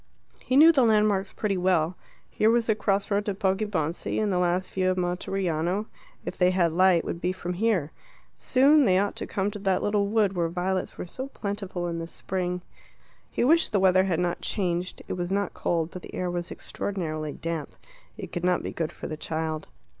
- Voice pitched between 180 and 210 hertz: Yes, medium, 185 Hz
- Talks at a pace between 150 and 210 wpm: Yes, average, 200 wpm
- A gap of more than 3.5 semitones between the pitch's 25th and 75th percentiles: No, narrow, 2.6 semitones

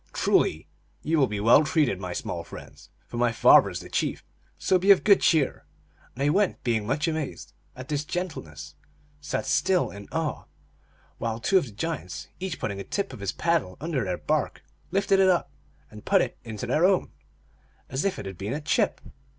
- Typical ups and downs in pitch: No, wide, 8.2 semitones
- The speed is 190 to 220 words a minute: Yes, fast, 205 wpm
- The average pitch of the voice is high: No, medium, 140 Hz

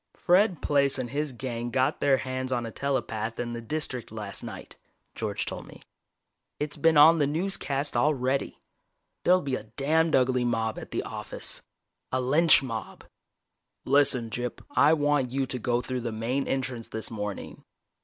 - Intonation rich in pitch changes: No, average, 3.4 semitones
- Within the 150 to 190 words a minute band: Yes, average, 165 wpm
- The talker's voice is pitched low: Yes, low, 130 Hz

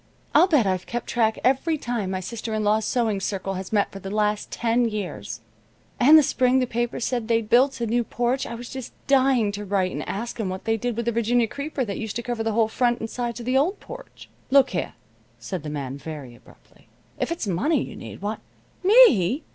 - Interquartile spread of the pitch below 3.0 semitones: No, average, 3.7 semitones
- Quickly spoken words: Yes, fast, 225 wpm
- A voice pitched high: Yes, high, 230 Hz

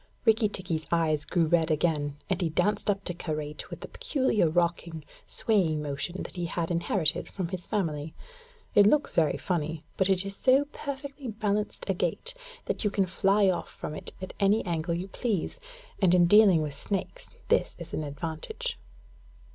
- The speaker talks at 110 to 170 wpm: No, average, 180 wpm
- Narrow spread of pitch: No, average, 4.3 semitones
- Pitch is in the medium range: Yes, medium, 180 Hz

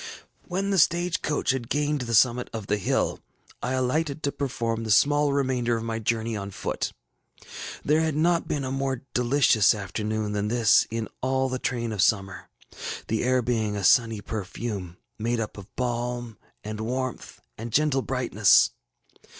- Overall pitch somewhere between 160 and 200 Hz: No, low, 120 Hz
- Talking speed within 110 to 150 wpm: No, average, 165 wpm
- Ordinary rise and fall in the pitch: Yes, average, 3.6 semitones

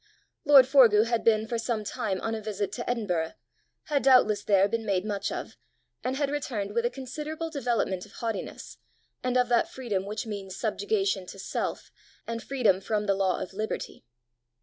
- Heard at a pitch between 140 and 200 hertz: No, high, 225 Hz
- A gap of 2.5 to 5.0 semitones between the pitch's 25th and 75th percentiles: Yes, average, 4.0 semitones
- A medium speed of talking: Yes, average, 180 wpm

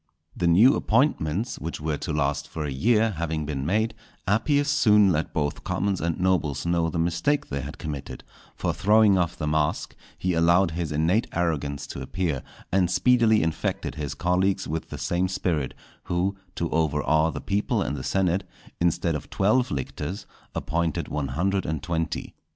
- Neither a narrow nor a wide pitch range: Yes, average, 4.2 semitones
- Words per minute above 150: Yes, average, 170 wpm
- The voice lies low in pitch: Yes, very low, 85 Hz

